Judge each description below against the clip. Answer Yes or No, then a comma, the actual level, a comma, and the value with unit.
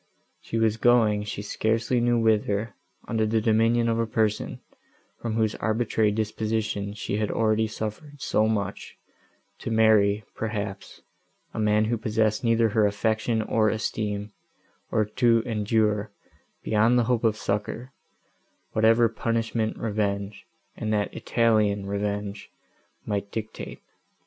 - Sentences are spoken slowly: Yes, slow, 130 wpm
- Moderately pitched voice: No, low, 110 Hz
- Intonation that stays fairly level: Yes, narrow, 1.4 semitones